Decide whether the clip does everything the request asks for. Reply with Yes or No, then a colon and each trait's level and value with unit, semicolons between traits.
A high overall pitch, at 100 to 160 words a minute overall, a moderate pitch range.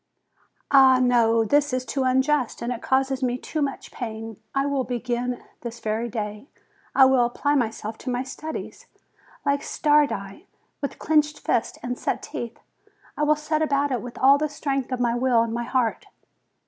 No: very high, 255 Hz; average, 175 wpm; average, 3.0 semitones